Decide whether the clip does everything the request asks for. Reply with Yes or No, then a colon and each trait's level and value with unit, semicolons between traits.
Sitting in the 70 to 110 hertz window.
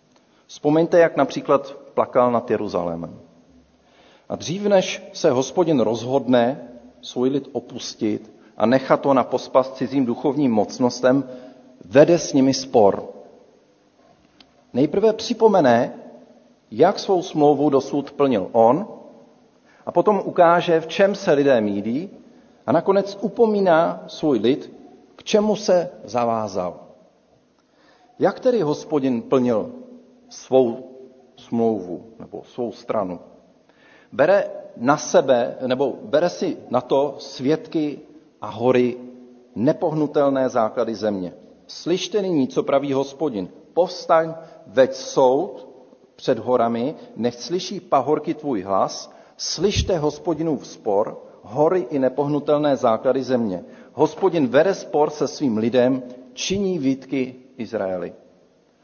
No: medium, 140 Hz